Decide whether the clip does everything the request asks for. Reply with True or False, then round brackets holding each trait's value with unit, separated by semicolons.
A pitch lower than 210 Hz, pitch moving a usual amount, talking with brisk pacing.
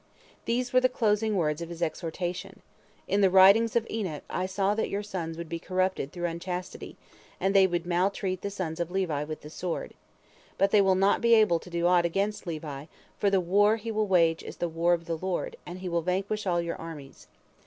True (185 Hz; 3.0 semitones; 215 wpm)